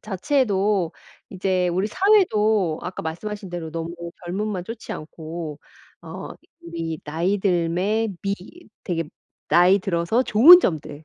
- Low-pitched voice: No, medium, 185 Hz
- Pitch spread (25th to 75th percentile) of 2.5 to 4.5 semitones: Yes, average, 3.9 semitones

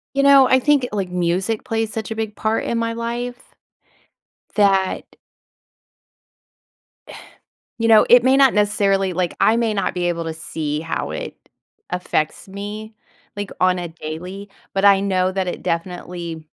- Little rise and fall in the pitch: No, average, 4.0 semitones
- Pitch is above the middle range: Yes, high, 200 Hz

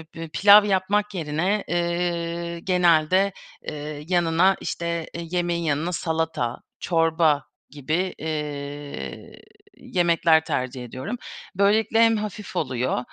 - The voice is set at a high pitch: No, medium, 170 Hz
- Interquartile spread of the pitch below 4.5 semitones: Yes, average, 3.5 semitones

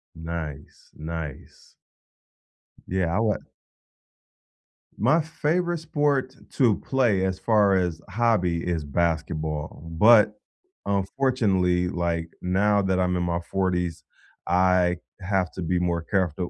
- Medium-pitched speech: No, very low, 90 Hz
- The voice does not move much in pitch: No, average, 3.7 semitones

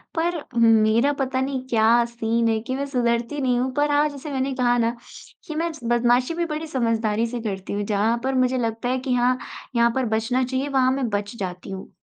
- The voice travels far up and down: No, narrow, 2.6 semitones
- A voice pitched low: No, high, 245 Hz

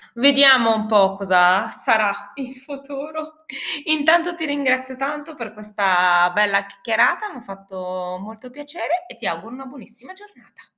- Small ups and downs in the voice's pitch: No, wide, 6.3 semitones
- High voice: Yes, high, 240 Hz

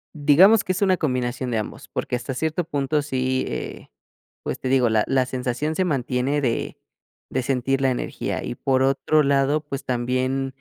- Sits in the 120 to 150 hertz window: Yes, low, 135 Hz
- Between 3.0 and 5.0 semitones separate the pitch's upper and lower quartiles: No, narrow, 2.6 semitones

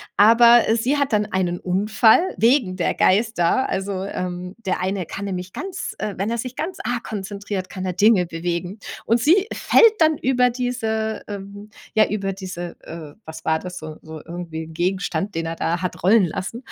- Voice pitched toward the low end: No, high, 200 Hz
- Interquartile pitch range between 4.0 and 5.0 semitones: Yes, average, 4.3 semitones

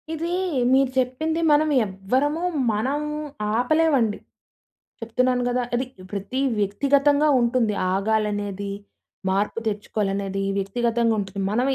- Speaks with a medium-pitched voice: No, high, 235 Hz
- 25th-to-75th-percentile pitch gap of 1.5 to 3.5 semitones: No, average, 5.0 semitones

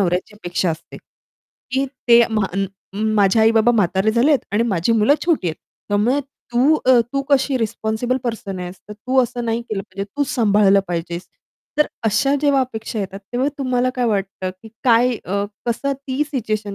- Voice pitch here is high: Yes, high, 225 Hz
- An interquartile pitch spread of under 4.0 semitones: No, average, 4.3 semitones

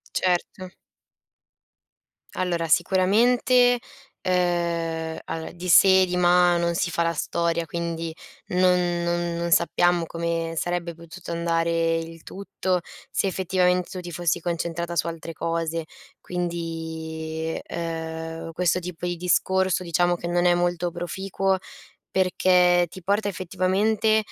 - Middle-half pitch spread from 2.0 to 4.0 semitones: No, narrow, 1.5 semitones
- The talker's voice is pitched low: No, medium, 175 Hz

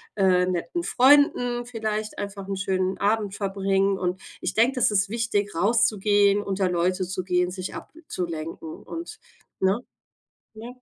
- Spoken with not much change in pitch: No, average, 3.1 semitones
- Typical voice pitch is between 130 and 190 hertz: No, high, 200 Hz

